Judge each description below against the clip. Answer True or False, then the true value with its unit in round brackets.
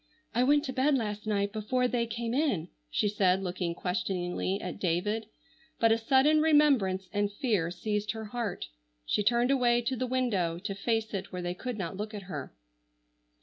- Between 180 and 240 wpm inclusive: True (185 wpm)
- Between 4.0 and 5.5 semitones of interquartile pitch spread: True (4.5 semitones)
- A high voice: True (210 Hz)